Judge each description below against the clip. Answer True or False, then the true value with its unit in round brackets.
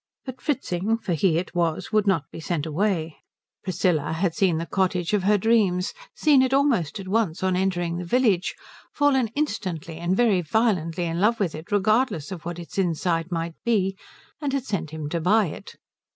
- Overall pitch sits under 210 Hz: True (185 Hz)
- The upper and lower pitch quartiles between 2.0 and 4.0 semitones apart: False (4.4 semitones)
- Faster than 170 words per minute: True (190 wpm)